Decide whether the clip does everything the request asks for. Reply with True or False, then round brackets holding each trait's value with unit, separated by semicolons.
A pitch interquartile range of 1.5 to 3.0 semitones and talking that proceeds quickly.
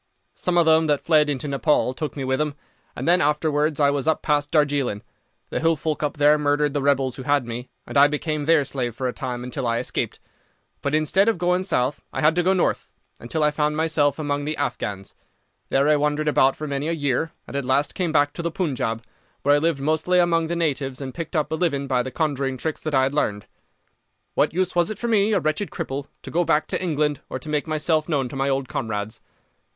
True (2.7 semitones; 235 wpm)